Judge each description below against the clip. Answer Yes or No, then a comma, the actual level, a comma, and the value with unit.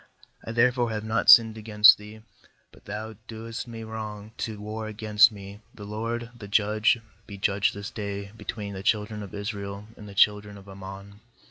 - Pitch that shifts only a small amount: Yes, narrow, 1.6 semitones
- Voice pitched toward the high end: No, low, 105 Hz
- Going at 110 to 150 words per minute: No, average, 175 wpm